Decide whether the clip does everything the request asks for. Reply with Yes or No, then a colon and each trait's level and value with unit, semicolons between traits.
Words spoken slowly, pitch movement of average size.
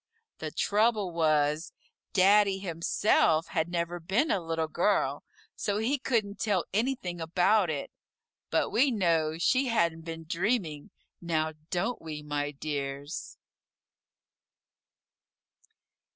Yes: slow, 110 wpm; average, 4.5 semitones